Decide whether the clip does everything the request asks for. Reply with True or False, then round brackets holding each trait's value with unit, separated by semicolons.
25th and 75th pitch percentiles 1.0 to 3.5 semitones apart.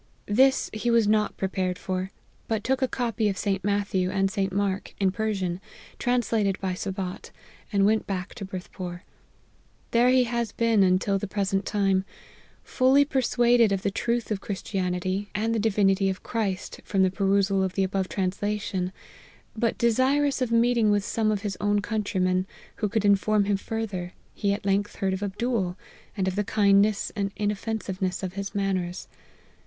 True (2.5 semitones)